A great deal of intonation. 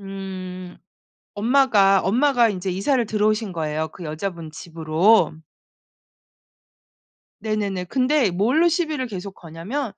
No: average, 4.9 semitones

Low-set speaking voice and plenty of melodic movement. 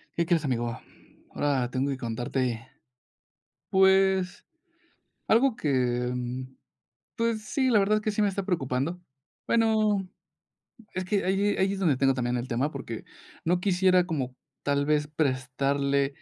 No: medium, 150 Hz; wide, 6.9 semitones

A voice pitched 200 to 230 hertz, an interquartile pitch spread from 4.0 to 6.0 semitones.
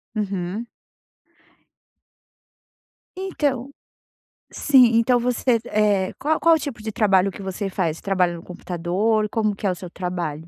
Yes: high, 205 Hz; average, 4.7 semitones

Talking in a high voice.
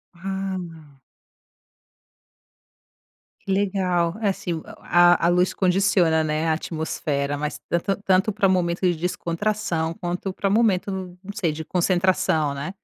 No: medium, 180 Hz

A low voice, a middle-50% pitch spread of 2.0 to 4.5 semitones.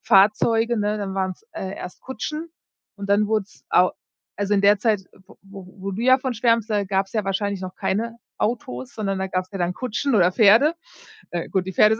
No: high, 205 Hz; average, 2.8 semitones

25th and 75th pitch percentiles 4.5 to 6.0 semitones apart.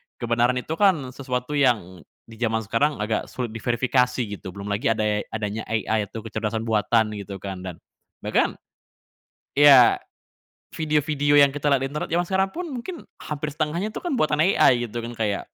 Yes: average, 5.2 semitones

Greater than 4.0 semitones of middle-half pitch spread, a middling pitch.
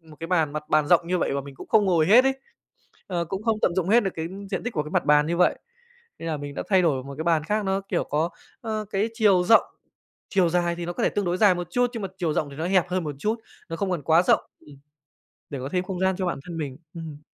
No: average, 3.7 semitones; medium, 175 Hz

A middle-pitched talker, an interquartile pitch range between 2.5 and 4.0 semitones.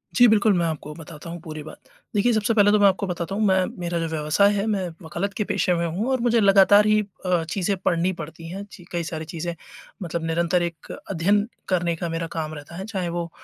Yes: medium, 175 Hz; average, 3.4 semitones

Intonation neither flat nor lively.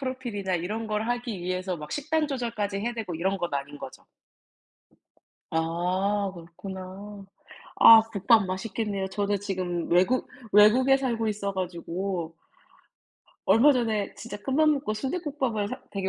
Yes: average, 4.2 semitones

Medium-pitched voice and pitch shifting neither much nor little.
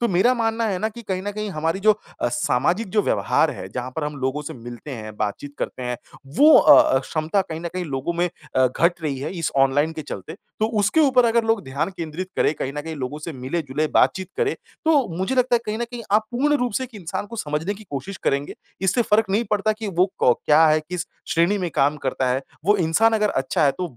No: medium, 175 Hz; wide, 6.9 semitones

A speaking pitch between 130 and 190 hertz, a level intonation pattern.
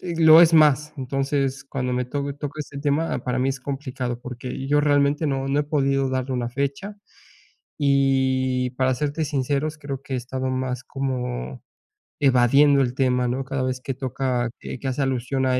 Yes: low, 135 Hz; narrow, 1.9 semitones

